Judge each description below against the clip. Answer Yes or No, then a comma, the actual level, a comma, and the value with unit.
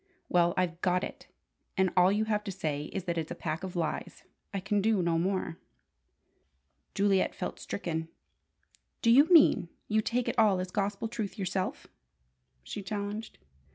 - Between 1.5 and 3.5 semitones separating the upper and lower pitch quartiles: Yes, average, 3.2 semitones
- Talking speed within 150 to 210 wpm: Yes, average, 165 wpm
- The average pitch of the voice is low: No, high, 190 Hz